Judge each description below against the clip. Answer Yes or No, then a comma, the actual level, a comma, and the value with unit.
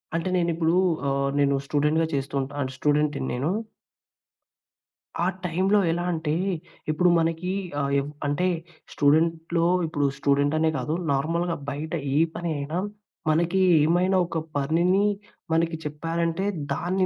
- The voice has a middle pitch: Yes, medium, 160 Hz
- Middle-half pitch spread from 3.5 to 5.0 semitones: No, average, 2.9 semitones